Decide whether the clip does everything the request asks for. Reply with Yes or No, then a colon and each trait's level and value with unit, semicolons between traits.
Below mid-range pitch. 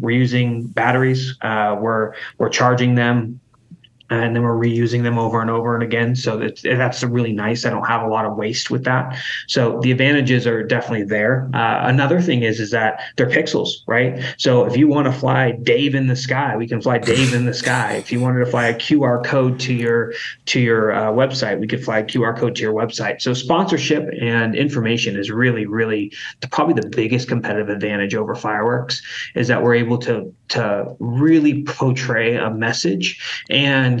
Yes: low, 120 Hz